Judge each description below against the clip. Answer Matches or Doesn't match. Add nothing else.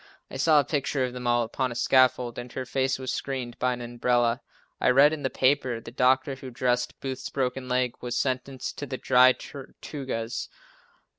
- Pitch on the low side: Matches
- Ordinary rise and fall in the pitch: Doesn't match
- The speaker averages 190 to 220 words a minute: Matches